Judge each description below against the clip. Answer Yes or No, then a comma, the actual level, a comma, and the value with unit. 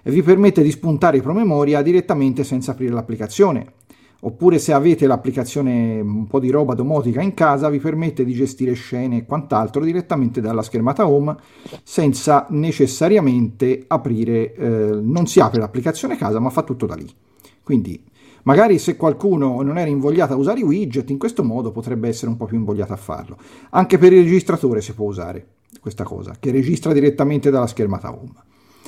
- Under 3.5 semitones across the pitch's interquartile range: No, average, 5.1 semitones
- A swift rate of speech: Yes, fast, 175 wpm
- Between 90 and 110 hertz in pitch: No, low, 135 Hz